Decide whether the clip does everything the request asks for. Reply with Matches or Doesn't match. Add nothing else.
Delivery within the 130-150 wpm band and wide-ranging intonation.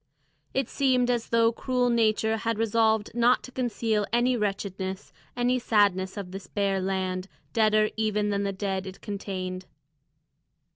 Doesn't match